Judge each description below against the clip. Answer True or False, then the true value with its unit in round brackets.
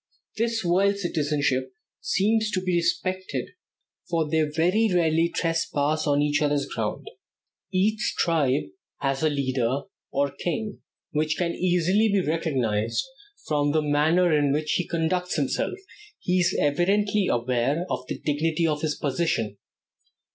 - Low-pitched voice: False (160 Hz)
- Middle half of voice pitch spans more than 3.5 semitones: True (4.0 semitones)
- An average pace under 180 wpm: True (140 wpm)